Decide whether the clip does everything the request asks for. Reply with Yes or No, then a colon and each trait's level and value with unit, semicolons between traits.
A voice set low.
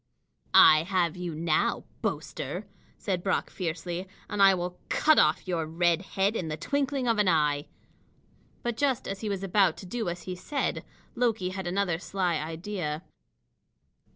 No: medium, 185 Hz